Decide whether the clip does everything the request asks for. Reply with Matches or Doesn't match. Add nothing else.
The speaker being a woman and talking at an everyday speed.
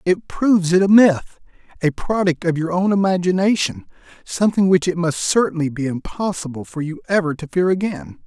Doesn't match